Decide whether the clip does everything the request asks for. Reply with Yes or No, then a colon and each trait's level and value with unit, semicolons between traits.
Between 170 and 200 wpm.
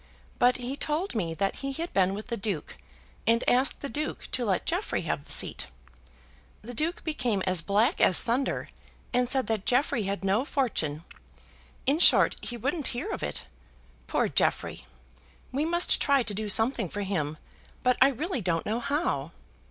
Yes: average, 175 wpm